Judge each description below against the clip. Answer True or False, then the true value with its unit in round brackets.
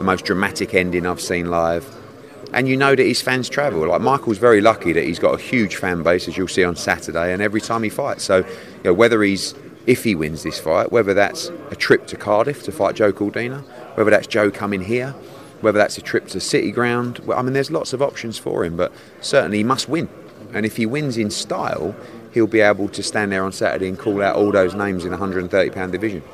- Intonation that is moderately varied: True (4.2 semitones)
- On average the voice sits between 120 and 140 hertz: False (105 Hz)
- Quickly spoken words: True (240 wpm)